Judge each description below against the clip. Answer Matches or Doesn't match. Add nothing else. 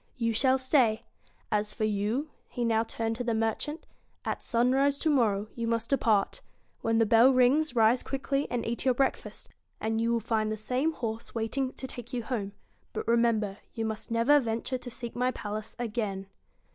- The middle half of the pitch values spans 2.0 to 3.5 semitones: Matches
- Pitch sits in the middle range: Doesn't match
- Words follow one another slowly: Doesn't match